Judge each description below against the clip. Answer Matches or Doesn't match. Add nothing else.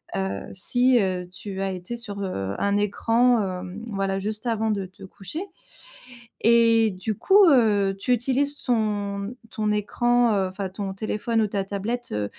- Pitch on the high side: Matches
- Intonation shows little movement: Doesn't match